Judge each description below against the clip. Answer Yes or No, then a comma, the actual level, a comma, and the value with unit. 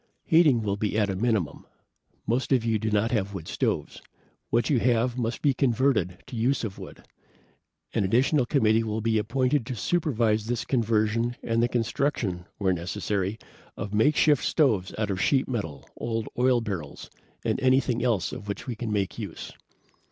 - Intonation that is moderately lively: Yes, average, 3.4 semitones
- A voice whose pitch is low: Yes, low, 115 Hz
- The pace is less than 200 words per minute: Yes, average, 175 wpm